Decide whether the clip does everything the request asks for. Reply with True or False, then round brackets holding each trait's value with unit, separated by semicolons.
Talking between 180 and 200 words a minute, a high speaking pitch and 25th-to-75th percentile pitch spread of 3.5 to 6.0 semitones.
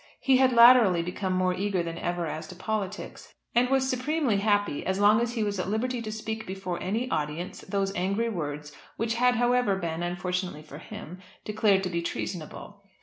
True (190 wpm; 200 Hz; 4.5 semitones)